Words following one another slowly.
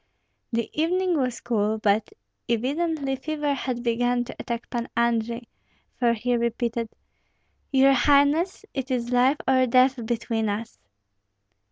Yes: slow, 130 wpm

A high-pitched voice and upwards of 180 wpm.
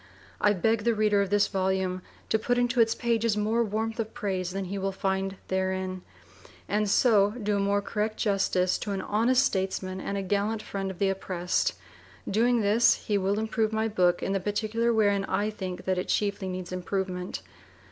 Yes: high, 200 Hz; average, 190 wpm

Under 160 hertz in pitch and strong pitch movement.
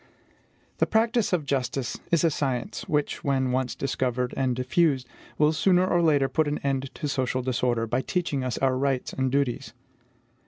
No: low, 135 Hz; average, 2.8 semitones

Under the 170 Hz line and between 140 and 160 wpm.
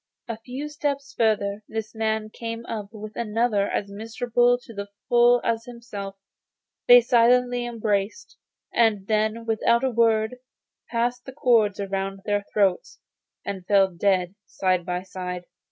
No: high, 220 Hz; average, 145 wpm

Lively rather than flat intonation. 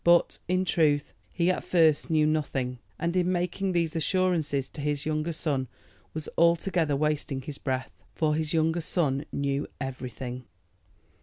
No: average, 3.4 semitones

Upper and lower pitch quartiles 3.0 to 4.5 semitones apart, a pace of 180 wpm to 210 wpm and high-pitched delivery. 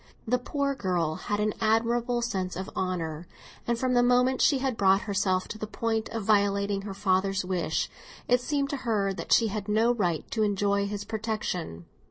Yes: average, 3.5 semitones; average, 190 wpm; high, 210 Hz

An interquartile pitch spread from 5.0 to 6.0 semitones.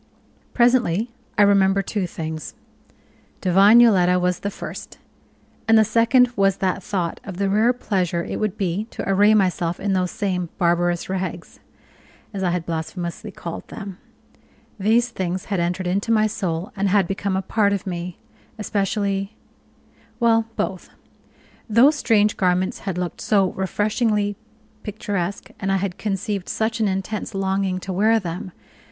No: average, 2.8 semitones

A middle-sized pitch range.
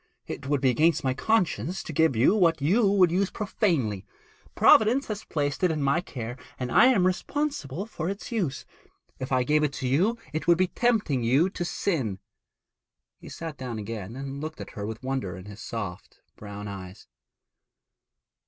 No: wide, 7.1 semitones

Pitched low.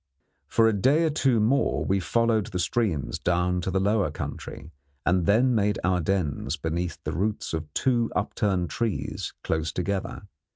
Yes: low, 100 Hz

